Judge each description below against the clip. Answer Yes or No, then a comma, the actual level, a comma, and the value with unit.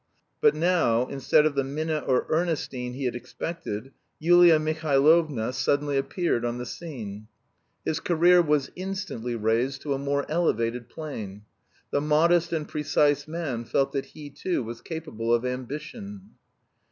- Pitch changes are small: No, average, 4.7 semitones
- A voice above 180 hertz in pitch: No, medium, 145 Hz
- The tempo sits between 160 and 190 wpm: No, average, 145 wpm